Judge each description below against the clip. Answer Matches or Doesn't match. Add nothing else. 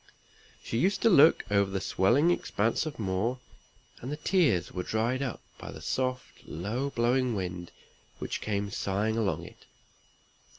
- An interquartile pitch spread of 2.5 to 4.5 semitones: Doesn't match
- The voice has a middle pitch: Doesn't match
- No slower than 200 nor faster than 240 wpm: Doesn't match